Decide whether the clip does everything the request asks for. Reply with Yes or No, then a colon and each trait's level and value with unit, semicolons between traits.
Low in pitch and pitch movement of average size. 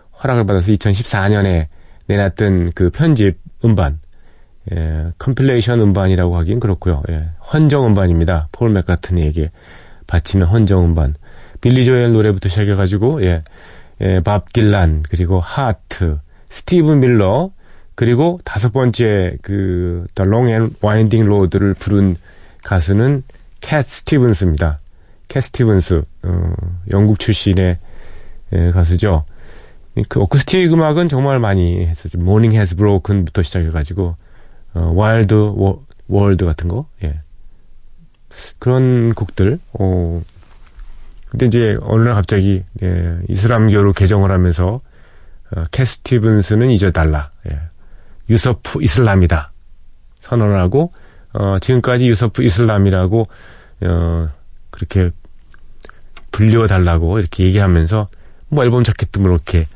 Yes: very low, 95 Hz; average, 4.5 semitones